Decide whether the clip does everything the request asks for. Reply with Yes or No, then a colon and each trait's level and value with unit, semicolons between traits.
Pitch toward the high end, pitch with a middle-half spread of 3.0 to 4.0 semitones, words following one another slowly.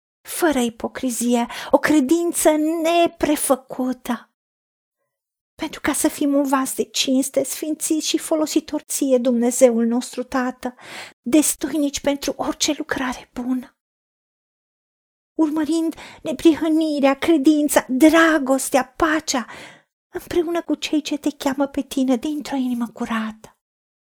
Yes: very high, 290 Hz; average, 3.5 semitones; slow, 100 wpm